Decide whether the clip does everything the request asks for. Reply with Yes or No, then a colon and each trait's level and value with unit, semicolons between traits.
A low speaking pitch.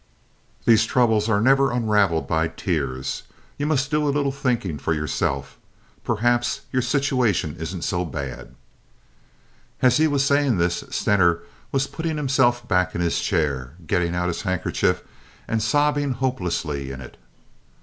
Yes: low, 110 Hz